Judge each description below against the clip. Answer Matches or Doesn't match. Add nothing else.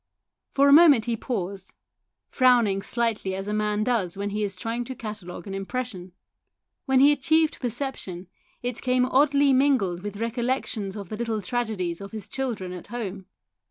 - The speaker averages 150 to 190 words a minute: Matches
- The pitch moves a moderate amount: Matches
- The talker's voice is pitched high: Matches